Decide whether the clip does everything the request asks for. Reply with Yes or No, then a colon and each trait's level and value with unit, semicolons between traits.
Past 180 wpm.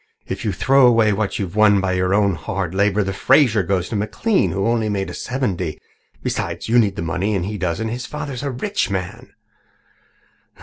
Yes: average, 200 wpm